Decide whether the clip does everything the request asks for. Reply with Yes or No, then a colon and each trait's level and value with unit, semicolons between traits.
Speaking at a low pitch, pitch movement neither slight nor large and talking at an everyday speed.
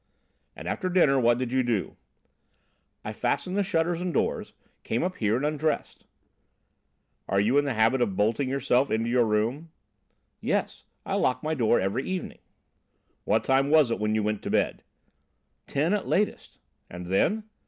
No: low, 130 Hz; wide, 6.0 semitones; average, 170 wpm